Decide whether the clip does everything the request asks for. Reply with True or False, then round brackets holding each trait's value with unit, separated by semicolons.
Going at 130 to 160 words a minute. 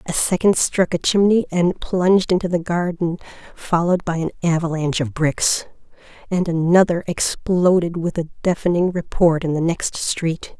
True (155 wpm)